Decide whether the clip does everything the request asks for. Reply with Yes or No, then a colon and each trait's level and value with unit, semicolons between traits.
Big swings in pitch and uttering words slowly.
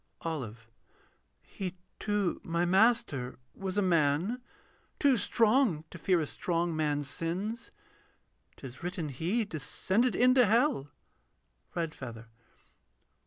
Yes: wide, 6.3 semitones; slow, 105 wpm